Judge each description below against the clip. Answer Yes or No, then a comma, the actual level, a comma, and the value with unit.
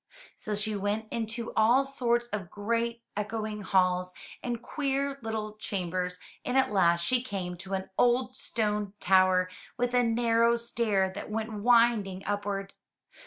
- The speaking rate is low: No, average, 145 wpm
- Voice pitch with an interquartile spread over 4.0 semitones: No, average, 3.3 semitones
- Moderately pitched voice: No, high, 215 Hz